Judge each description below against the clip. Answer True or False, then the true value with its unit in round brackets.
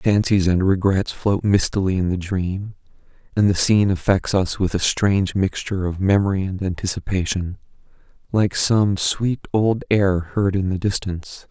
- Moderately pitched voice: False (95 Hz)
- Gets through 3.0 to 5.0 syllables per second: True (4.7 syllables/s)